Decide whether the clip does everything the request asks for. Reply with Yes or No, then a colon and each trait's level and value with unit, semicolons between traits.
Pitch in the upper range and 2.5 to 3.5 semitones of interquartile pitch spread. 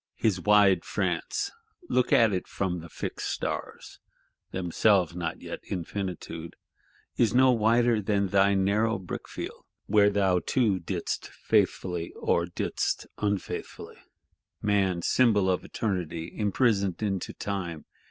No: low, 100 Hz; average, 3.0 semitones